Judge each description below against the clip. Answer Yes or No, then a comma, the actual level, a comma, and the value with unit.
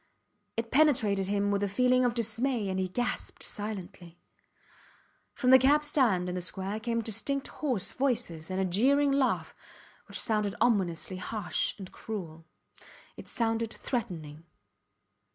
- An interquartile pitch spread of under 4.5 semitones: No, average, 4.9 semitones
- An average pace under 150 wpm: Yes, average, 140 wpm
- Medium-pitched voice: No, high, 220 Hz